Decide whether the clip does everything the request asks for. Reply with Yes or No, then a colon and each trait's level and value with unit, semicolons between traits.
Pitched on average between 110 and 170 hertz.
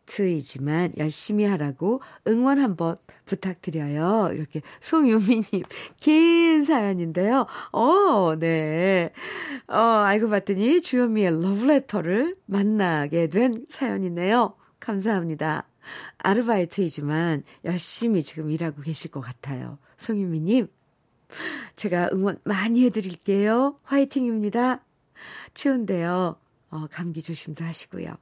No: high, 195 Hz